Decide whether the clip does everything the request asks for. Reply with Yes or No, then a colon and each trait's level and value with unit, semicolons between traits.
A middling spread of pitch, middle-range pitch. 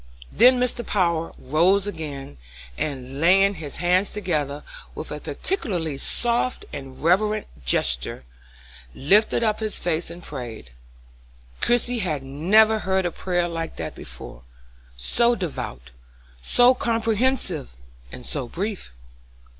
No: wide, 7.0 semitones; medium, 175 Hz